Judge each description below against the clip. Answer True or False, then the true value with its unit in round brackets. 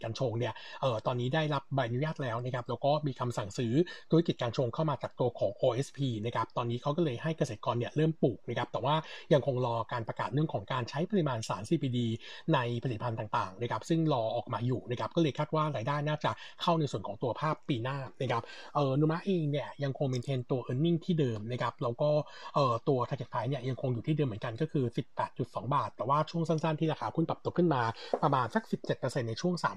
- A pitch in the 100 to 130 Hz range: False (140 Hz)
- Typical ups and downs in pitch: True (4.0 semitones)